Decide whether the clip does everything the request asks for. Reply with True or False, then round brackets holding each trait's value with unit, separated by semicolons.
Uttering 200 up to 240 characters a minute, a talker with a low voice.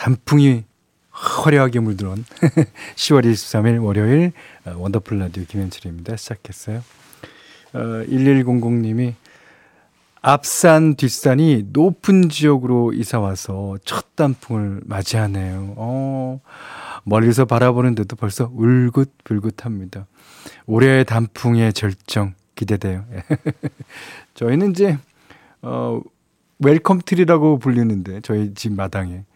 True (230 characters per minute; 115 Hz)